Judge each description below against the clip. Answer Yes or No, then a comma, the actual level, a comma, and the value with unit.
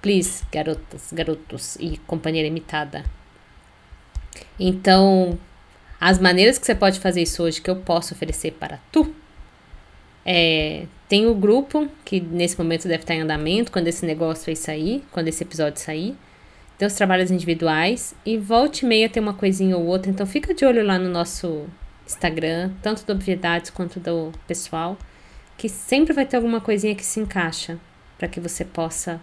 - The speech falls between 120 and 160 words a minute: No, average, 170 wpm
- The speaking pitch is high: No, medium, 180 Hz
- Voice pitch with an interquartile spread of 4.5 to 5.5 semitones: No, average, 4.1 semitones